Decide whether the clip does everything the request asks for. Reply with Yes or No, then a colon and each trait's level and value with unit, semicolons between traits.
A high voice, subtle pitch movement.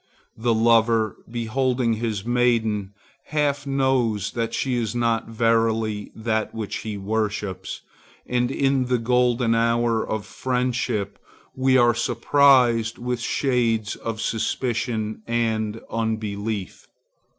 No: low, 115 Hz; narrow, 2.0 semitones